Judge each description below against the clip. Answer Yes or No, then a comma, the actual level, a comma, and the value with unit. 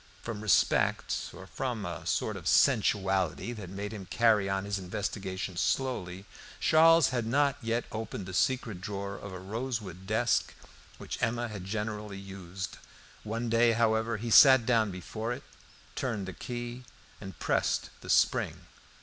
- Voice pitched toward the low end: Yes, low, 105 Hz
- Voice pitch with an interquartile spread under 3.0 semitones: No, average, 3.4 semitones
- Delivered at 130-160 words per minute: Yes, average, 150 wpm